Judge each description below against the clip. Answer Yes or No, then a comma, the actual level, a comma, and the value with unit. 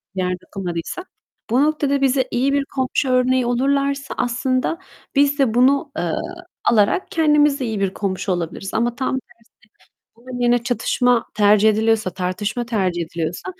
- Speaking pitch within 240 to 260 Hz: Yes, high, 245 Hz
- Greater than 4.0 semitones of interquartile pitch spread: Yes, average, 5.1 semitones